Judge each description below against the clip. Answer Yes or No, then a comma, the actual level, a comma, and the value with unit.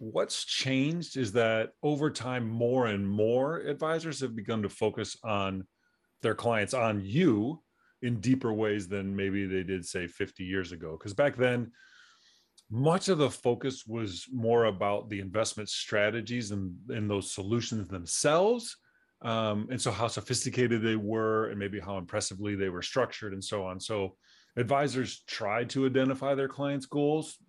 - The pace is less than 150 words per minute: No, average, 160 wpm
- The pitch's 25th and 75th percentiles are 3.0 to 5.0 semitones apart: Yes, average, 4.3 semitones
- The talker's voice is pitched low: Yes, low, 115 Hz